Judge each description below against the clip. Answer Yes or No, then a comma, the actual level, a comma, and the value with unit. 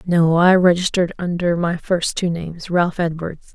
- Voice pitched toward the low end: No, medium, 170 Hz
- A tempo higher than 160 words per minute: No, average, 150 wpm